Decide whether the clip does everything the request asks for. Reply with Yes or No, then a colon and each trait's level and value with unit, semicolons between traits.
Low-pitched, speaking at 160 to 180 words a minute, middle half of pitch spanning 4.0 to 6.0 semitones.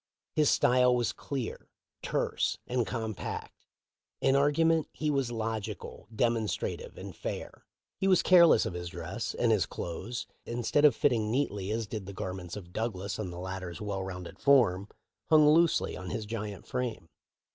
Yes: low, 110 Hz; average, 165 wpm; wide, 5.4 semitones